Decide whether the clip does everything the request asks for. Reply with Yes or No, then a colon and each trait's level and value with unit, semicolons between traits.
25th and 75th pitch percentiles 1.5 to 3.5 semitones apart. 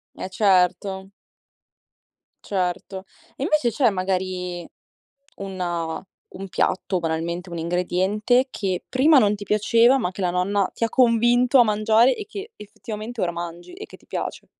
No: average, 4.5 semitones